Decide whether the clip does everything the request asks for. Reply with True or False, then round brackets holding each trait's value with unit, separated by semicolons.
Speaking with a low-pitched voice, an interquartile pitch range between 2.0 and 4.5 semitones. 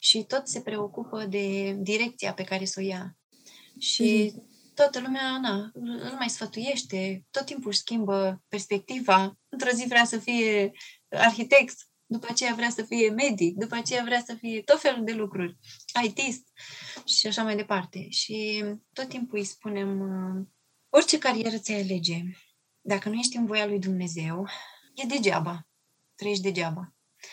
False (215 Hz; 3.7 semitones)